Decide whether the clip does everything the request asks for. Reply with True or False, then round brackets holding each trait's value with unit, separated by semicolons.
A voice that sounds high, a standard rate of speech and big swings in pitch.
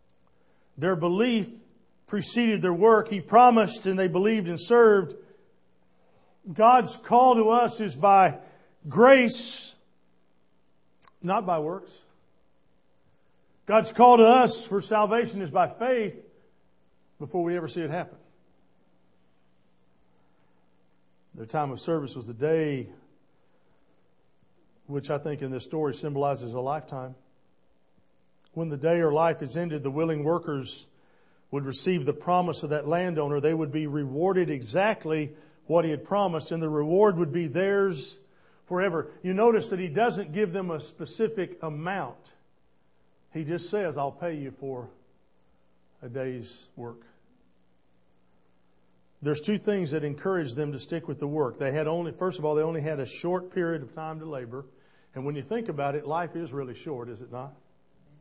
False (155 Hz; 150 wpm; 7.2 semitones)